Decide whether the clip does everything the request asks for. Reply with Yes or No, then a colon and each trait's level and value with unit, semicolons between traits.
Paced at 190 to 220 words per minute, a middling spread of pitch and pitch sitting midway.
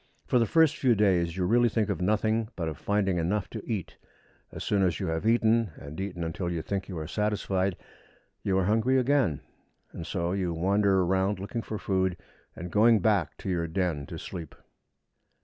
No: average, 195 wpm; average, 3.6 semitones; very low, 95 Hz